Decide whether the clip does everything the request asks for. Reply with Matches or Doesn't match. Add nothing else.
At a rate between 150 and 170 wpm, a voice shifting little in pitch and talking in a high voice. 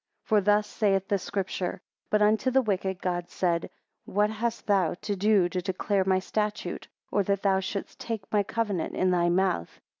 Doesn't match